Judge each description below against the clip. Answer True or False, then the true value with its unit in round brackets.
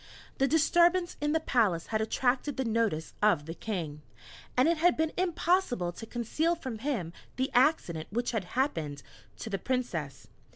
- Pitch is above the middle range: True (245 Hz)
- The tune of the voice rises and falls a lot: True (8.9 semitones)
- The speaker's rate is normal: True (165 wpm)